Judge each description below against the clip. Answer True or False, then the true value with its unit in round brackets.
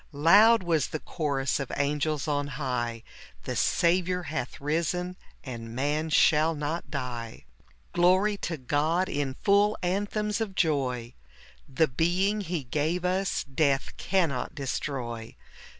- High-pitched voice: False (155 Hz)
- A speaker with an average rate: False (130 wpm)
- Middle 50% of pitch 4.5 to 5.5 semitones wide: True (4.9 semitones)